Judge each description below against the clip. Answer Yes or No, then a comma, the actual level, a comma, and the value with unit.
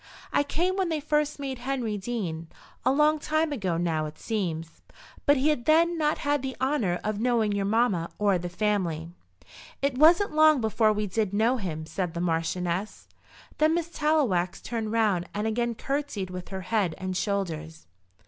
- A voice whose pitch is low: No, high, 220 Hz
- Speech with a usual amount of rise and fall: No, wide, 7.9 semitones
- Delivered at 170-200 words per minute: Yes, average, 175 wpm